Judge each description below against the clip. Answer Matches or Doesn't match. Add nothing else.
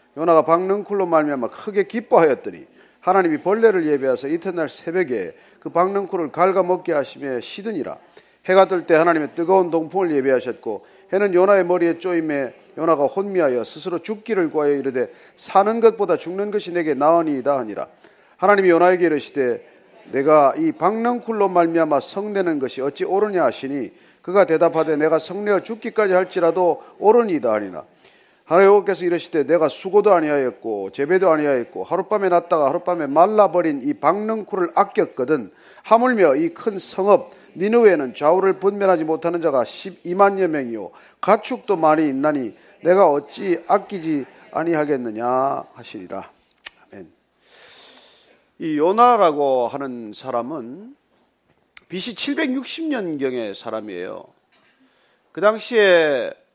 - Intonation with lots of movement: Doesn't match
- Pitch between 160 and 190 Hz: Matches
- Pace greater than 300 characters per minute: Matches